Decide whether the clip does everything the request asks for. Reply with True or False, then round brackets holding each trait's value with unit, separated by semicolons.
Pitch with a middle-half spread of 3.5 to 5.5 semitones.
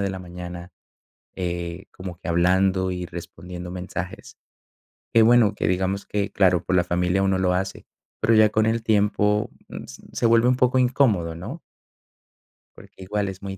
False (2.7 semitones)